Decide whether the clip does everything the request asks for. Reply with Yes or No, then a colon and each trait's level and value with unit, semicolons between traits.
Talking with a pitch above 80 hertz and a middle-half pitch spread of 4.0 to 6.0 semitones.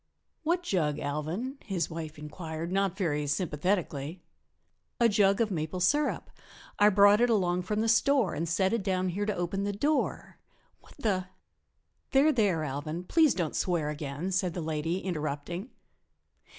Yes: medium, 185 Hz; average, 4.7 semitones